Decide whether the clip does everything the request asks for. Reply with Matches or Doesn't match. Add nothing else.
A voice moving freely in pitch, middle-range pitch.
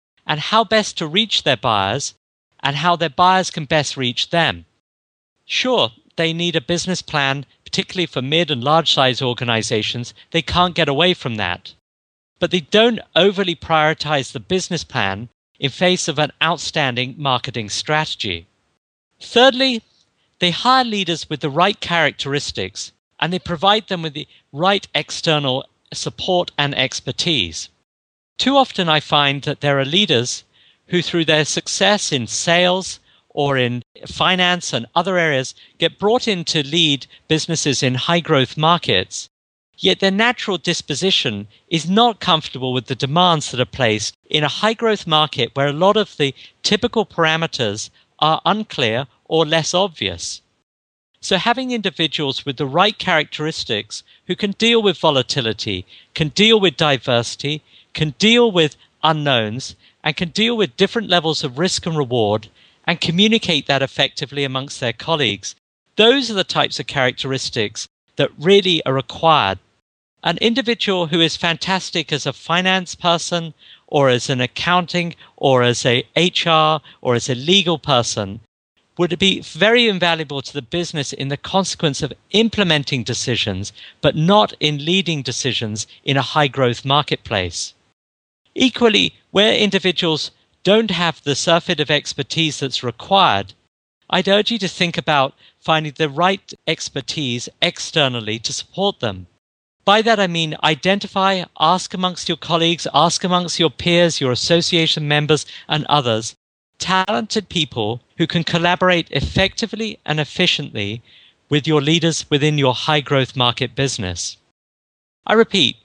Matches